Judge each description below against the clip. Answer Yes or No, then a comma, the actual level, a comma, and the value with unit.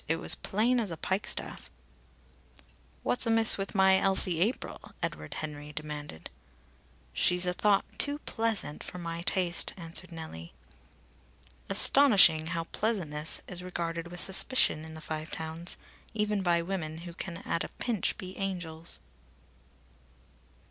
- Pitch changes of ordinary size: Yes, average, 3.4 semitones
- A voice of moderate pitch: Yes, medium, 175 Hz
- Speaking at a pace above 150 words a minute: No, slow, 135 wpm